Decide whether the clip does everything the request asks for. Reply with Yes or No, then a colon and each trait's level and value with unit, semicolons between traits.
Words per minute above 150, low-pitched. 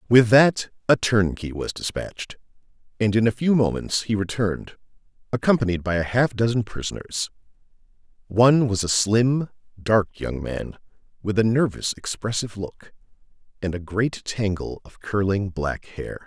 No: average, 145 wpm; low, 110 Hz